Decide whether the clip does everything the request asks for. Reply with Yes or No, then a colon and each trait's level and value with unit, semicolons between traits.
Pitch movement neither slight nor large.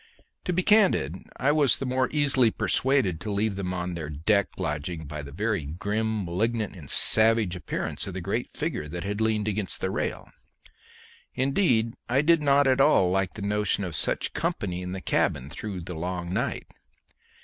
No: wide, 6.0 semitones